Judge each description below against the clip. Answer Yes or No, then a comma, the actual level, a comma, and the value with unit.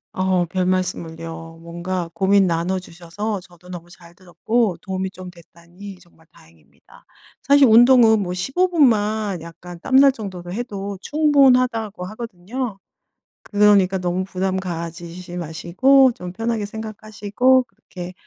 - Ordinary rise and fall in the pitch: Yes, average, 4.1 semitones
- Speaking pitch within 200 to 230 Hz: No, high, 190 Hz